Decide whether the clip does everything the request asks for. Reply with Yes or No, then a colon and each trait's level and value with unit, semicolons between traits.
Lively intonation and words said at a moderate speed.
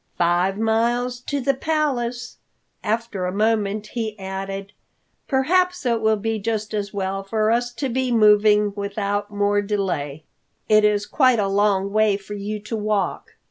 No: narrow, 2.6 semitones; average, 155 wpm